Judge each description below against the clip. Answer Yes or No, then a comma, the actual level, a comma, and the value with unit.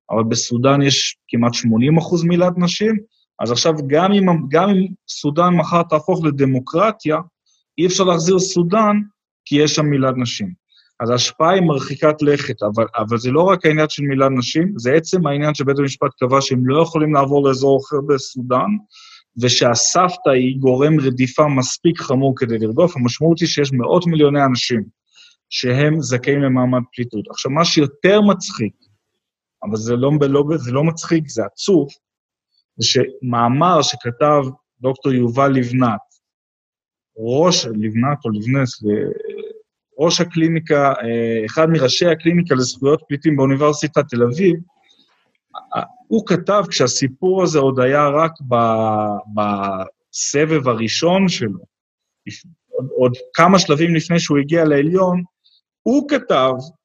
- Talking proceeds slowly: No, average, 130 wpm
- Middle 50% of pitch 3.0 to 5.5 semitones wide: Yes, average, 5.1 semitones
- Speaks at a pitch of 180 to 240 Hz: No, medium, 145 Hz